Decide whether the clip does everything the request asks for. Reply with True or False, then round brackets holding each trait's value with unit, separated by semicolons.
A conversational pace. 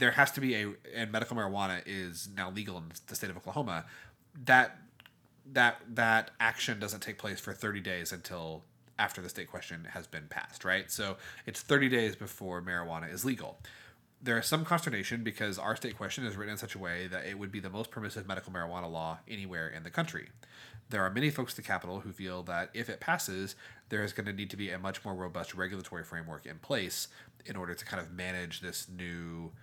False (215 wpm)